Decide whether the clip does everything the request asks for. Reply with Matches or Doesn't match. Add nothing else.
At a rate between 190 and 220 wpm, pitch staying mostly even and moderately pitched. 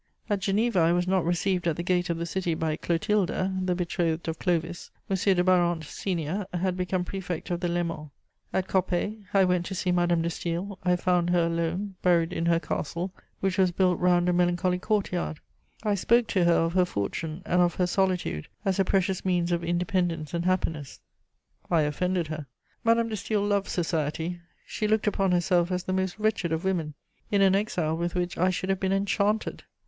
Matches